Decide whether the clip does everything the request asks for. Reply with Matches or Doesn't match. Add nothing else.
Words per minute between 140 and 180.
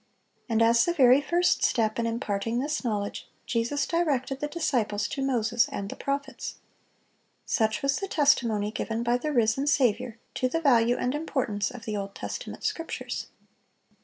Matches